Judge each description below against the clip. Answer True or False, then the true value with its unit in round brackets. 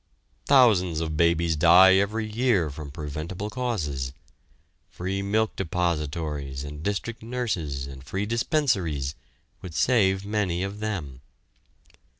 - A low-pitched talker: True (90 Hz)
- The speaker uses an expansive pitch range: True (5.8 semitones)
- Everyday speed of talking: False (115 wpm)